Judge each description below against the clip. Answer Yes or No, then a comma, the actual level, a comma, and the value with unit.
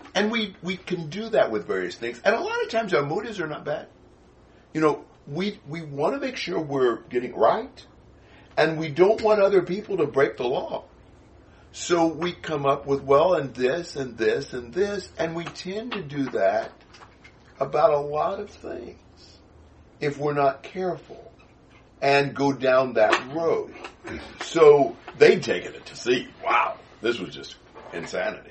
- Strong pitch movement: Yes, wide, 6.4 semitones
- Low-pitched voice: No, medium, 160 Hz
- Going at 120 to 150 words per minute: No, average, 175 wpm